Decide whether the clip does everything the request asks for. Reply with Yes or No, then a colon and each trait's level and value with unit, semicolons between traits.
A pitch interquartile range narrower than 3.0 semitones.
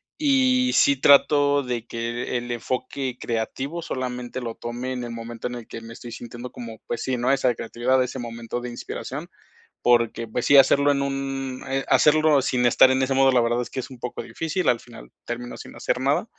Yes: narrow, 2.4 semitones